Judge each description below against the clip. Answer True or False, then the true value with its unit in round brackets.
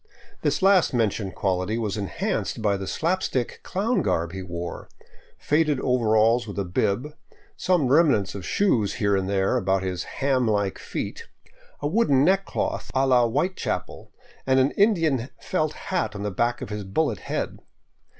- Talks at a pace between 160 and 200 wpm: True (170 wpm)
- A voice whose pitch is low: True (120 Hz)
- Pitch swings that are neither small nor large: False (7.2 semitones)